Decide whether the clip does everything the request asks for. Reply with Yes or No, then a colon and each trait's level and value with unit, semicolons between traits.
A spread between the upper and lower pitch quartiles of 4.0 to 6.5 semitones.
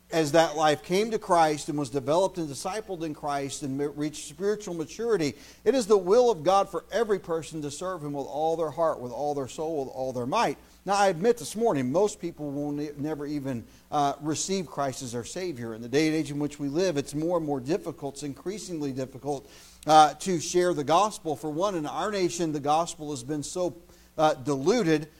No: average, 3.6 semitones